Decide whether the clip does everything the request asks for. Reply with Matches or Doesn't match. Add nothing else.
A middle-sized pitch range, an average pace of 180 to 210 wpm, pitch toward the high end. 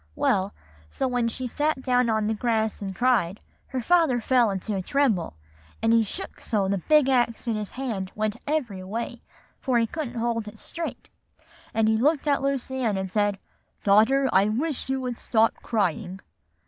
Matches